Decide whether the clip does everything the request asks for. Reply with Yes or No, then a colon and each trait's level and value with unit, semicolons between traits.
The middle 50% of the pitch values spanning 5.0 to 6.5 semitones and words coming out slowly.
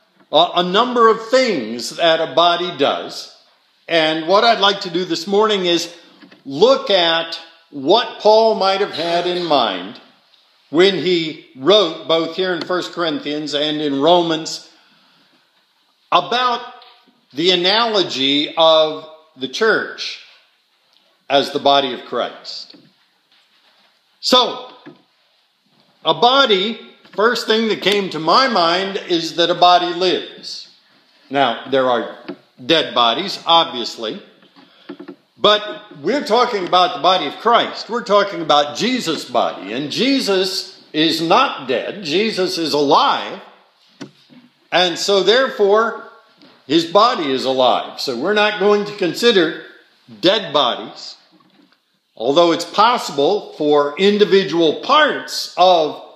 Yes: wide, 5.4 semitones; slow, 120 wpm